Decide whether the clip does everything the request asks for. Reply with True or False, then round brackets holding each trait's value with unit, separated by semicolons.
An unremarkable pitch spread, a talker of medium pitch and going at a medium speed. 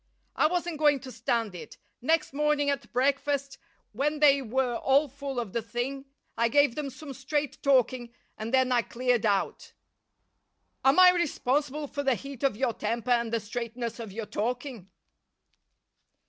False (3.4 semitones; 260 Hz; 160 wpm)